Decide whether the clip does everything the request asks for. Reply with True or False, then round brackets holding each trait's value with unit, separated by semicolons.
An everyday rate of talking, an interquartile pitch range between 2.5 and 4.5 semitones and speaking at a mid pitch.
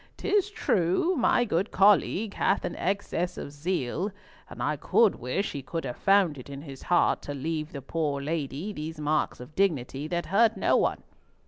False (185 wpm; 5.6 semitones; 165 Hz)